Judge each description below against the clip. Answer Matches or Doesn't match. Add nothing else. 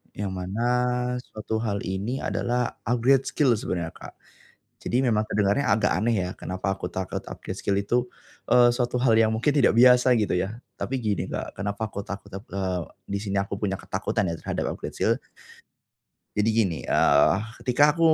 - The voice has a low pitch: Matches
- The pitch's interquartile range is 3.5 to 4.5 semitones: Matches